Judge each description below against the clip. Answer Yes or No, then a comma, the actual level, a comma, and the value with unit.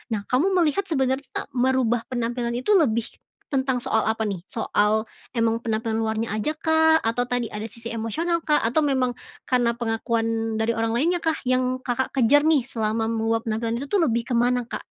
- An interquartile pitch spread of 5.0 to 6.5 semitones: No, average, 2.8 semitones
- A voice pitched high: Yes, high, 240 Hz